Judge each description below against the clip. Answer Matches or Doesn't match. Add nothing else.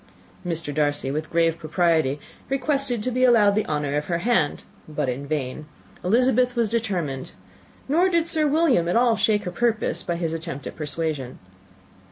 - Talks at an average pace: Matches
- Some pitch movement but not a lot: Doesn't match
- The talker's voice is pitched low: Doesn't match